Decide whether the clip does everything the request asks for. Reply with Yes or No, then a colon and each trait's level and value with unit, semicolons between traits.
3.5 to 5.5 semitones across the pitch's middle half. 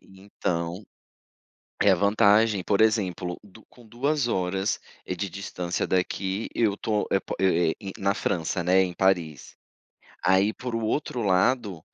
No: average, 3.0 semitones